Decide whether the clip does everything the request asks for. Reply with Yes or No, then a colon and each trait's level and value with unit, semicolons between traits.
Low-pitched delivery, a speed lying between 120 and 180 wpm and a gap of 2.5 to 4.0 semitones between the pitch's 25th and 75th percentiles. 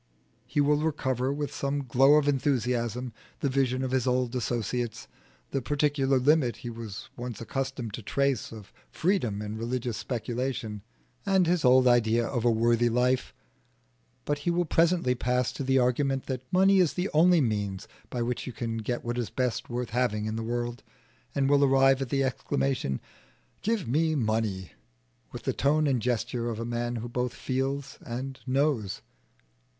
Yes: low, 125 Hz; average, 170 wpm; average, 2.8 semitones